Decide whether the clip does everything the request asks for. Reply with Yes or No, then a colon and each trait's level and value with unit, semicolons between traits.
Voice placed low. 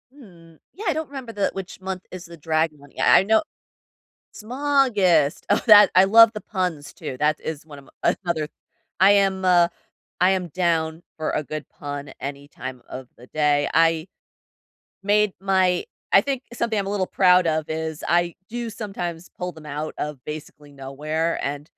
No: medium, 170 Hz